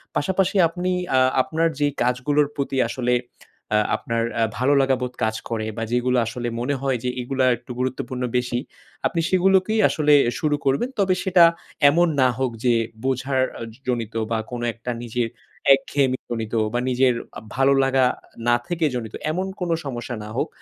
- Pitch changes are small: No, average, 3.5 semitones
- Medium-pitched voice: No, low, 130 Hz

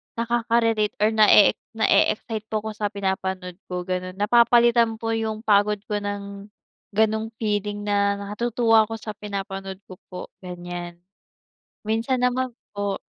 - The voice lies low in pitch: No, high, 210 Hz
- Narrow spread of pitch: Yes, narrow, 2.1 semitones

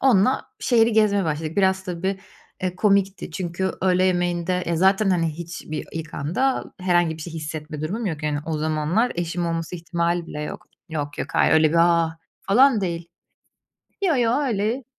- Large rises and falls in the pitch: No, average, 3.3 semitones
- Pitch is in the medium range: Yes, medium, 175 Hz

